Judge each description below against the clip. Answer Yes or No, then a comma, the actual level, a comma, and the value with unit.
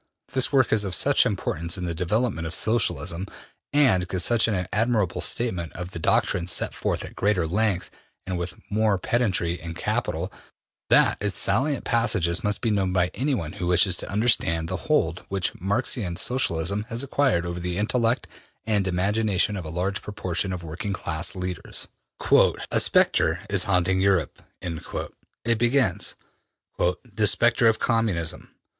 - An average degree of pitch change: Yes, average, 4.2 semitones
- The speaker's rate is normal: Yes, average, 155 wpm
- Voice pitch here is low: Yes, very low, 95 Hz